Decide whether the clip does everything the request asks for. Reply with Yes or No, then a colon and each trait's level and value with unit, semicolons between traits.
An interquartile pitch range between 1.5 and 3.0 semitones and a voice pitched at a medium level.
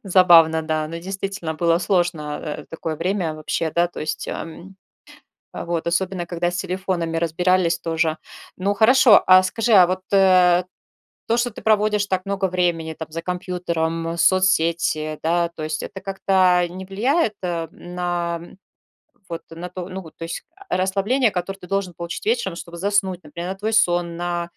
Yes: narrow, 2.4 semitones; medium, 175 Hz